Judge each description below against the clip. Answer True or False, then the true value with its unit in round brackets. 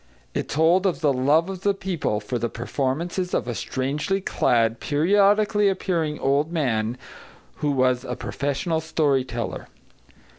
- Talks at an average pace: True (145 wpm)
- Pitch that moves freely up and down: True (5.7 semitones)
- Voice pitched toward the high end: False (150 Hz)